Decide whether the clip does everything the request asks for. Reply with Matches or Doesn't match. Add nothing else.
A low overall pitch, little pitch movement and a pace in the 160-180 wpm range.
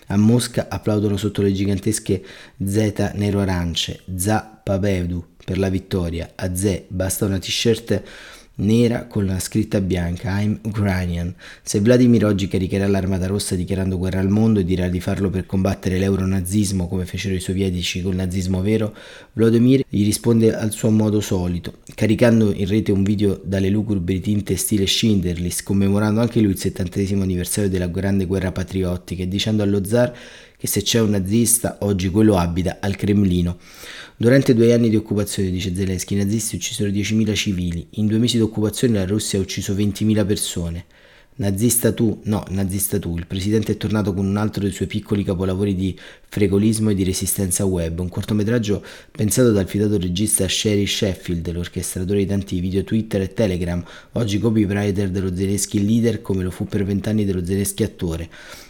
Matches